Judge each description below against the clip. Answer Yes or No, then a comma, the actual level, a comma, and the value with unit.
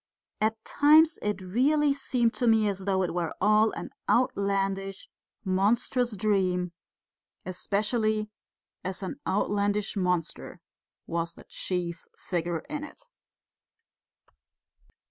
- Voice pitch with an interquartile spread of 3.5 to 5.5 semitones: Yes, average, 3.8 semitones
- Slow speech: Yes, slow, 105 wpm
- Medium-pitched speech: No, high, 205 Hz